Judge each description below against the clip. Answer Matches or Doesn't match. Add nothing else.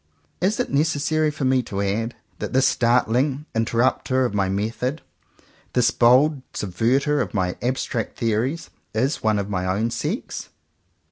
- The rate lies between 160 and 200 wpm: Doesn't match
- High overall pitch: Doesn't match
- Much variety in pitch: Doesn't match